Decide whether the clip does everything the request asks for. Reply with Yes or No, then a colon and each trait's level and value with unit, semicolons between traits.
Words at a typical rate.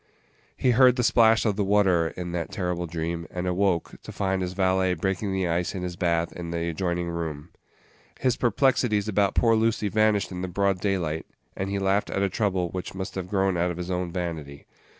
No: fast, 210 wpm